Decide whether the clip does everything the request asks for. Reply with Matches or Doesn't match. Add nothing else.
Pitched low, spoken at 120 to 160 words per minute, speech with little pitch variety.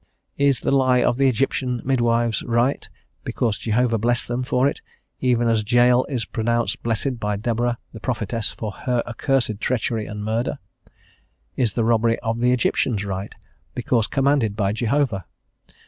Matches